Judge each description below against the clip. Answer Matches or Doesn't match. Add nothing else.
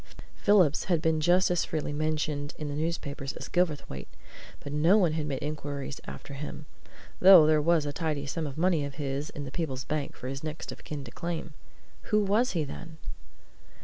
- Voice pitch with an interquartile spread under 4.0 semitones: Matches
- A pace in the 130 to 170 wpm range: Doesn't match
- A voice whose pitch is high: Doesn't match